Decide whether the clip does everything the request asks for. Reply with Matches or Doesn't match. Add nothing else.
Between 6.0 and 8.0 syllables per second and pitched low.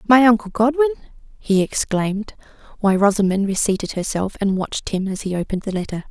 Doesn't match